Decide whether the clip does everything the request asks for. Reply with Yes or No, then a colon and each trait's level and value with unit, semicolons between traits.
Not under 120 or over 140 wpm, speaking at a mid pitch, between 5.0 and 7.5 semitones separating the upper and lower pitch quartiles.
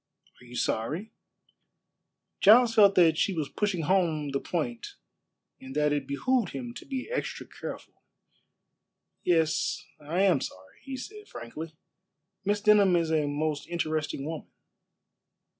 Yes: slow, 135 wpm; medium, 160 Hz; wide, 5.6 semitones